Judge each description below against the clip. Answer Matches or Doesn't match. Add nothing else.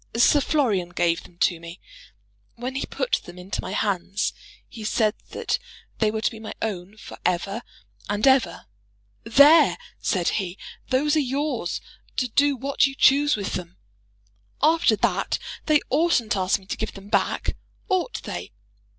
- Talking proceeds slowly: Doesn't match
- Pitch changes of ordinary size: Doesn't match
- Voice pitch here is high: Matches